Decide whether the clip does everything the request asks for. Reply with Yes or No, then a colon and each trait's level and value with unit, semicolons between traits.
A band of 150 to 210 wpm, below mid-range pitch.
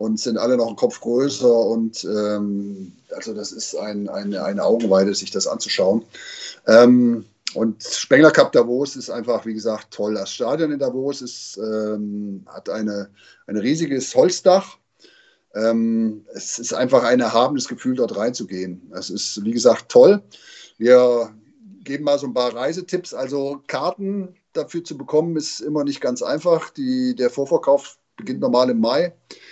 Yes: average, 160 wpm; low, 125 Hz